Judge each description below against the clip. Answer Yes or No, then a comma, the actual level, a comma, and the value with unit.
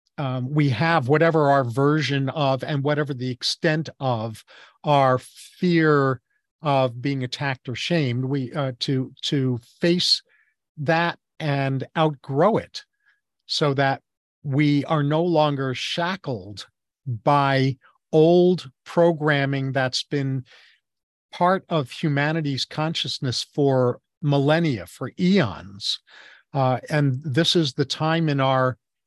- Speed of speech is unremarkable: No, slow, 115 wpm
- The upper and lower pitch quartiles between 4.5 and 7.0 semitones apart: No, average, 3.2 semitones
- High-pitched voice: No, medium, 140 Hz